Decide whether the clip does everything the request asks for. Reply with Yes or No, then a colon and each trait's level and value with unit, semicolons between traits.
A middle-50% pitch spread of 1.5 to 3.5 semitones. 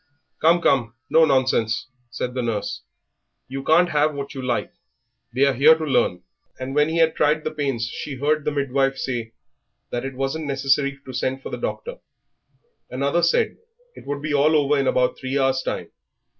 Yes: average, 2.8 semitones